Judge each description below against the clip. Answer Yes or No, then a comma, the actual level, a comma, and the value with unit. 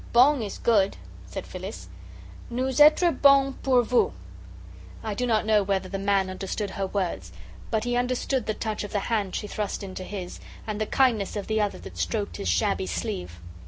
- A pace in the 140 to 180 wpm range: No, average, 195 wpm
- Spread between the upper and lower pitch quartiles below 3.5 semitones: No, average, 3.8 semitones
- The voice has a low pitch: No, high, 215 Hz